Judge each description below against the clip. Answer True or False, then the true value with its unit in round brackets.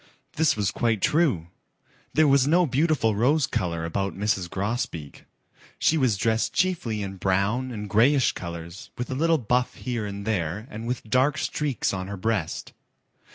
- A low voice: True (110 Hz)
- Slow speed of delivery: False (160 wpm)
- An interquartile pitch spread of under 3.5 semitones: False (5.3 semitones)